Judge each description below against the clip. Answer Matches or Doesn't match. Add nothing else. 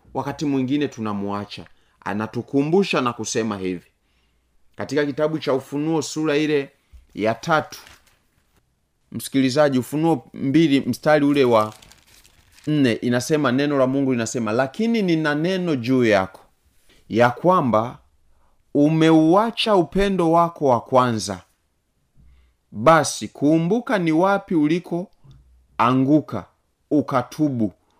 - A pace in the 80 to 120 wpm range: Matches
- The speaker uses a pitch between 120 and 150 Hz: Matches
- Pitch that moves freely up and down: Matches